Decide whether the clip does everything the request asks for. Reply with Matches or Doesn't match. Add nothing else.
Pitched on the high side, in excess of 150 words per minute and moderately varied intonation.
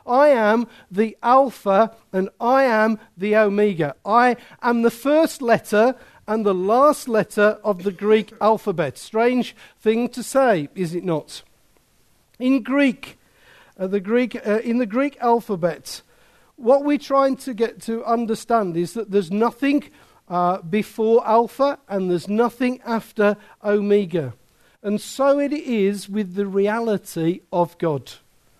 Doesn't match